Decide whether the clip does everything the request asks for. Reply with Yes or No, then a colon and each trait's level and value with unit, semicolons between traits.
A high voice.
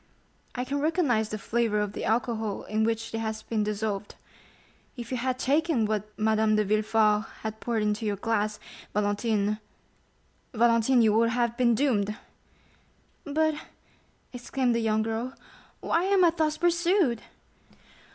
Yes: high, 225 Hz